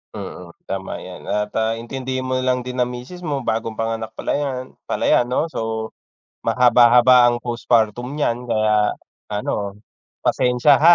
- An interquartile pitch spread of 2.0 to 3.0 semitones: Yes, narrow, 2.4 semitones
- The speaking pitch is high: No, low, 120 Hz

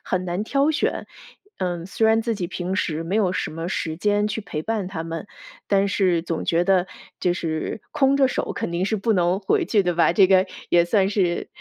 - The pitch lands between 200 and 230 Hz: No, medium, 185 Hz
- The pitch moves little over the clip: No, average, 3.5 semitones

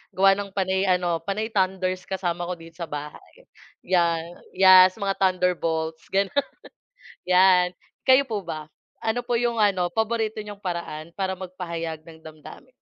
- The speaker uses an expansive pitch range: No, average, 2.8 semitones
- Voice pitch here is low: No, medium, 185 Hz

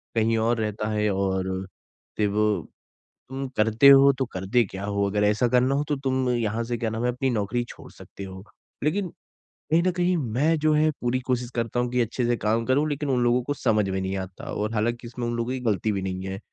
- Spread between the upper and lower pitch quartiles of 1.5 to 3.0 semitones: No, average, 3.6 semitones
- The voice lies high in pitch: No, low, 120 Hz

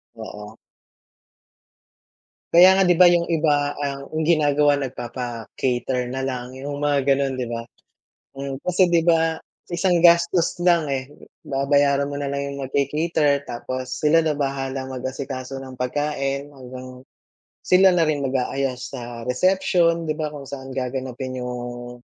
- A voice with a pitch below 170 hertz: Yes, medium, 140 Hz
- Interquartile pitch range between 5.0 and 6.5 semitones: No, average, 3.4 semitones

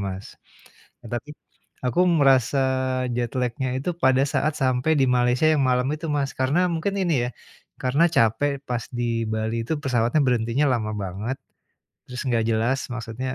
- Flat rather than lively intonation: No, average, 3.4 semitones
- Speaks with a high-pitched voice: No, low, 125 Hz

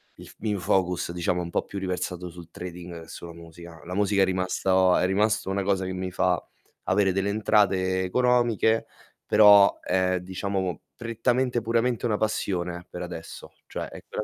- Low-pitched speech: Yes, very low, 95 Hz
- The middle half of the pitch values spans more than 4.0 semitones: No, narrow, 2.6 semitones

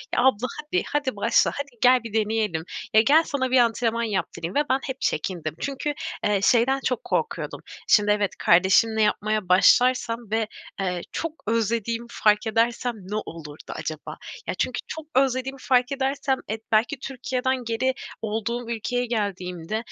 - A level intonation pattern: No, average, 3.8 semitones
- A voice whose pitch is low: No, high, 230 Hz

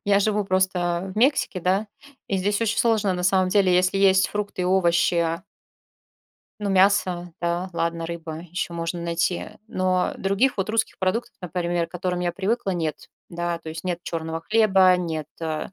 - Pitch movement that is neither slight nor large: No, narrow, 2.3 semitones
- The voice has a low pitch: No, medium, 185 Hz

